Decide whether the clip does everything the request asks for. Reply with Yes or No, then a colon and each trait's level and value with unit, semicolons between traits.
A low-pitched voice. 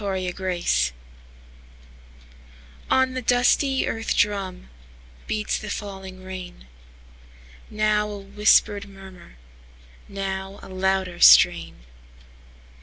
No: high, 190 Hz